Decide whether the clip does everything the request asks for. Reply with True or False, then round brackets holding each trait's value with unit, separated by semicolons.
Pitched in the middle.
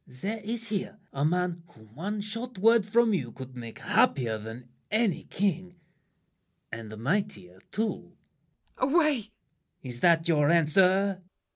True (180 Hz)